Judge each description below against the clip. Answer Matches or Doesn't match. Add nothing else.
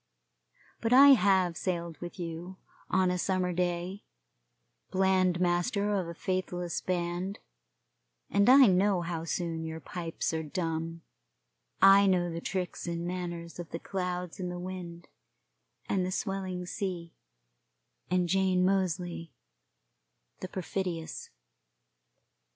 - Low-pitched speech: Doesn't match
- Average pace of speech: Doesn't match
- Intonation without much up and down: Matches